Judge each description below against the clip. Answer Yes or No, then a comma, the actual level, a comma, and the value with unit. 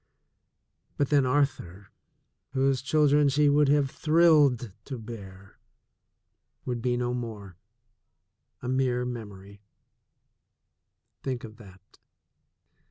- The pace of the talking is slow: Yes, slow, 100 wpm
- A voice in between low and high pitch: No, low, 125 Hz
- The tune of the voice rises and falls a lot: No, average, 4.6 semitones